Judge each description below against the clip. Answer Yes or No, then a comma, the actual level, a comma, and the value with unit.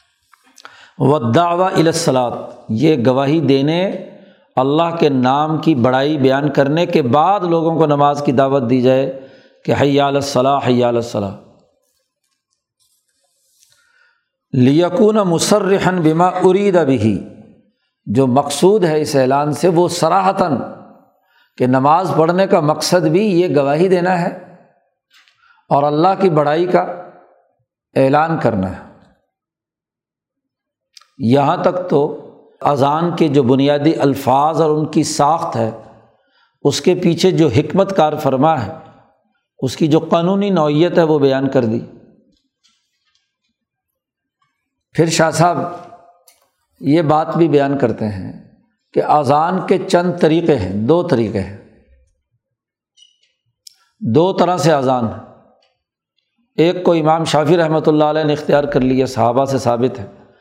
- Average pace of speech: Yes, average, 125 wpm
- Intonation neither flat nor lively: Yes, average, 4.8 semitones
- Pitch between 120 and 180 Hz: Yes, medium, 155 Hz